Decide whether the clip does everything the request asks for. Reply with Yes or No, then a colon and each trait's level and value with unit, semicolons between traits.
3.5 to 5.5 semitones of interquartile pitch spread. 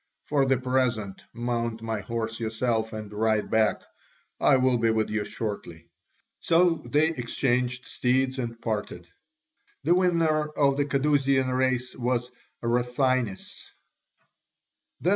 No: average, 3.1 semitones